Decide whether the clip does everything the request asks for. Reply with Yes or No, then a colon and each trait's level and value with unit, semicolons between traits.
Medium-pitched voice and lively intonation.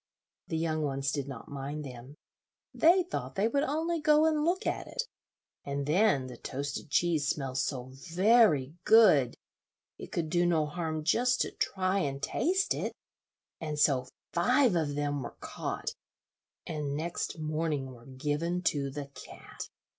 Yes: medium, 155 Hz; wide, 5.8 semitones